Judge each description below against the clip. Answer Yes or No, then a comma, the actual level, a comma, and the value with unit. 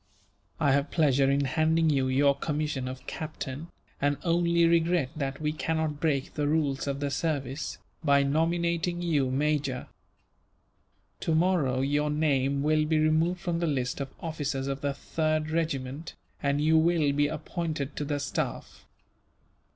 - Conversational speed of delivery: Yes, average, 150 wpm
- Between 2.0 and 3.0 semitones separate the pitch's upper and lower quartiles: Yes, narrow, 2.6 semitones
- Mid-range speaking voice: Yes, medium, 150 Hz